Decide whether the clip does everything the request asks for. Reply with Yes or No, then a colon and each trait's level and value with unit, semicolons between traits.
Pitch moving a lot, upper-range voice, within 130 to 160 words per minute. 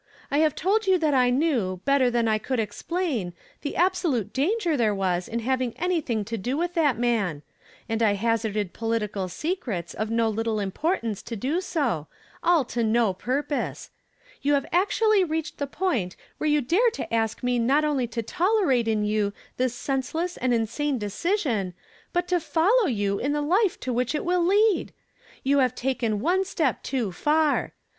No: wide, 6.7 semitones; very high, 255 Hz; average, 180 wpm